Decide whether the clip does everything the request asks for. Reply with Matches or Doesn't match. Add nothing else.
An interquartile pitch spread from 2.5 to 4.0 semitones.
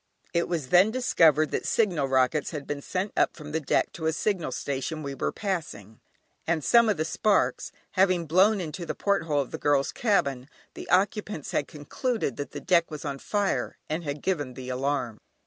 Doesn't match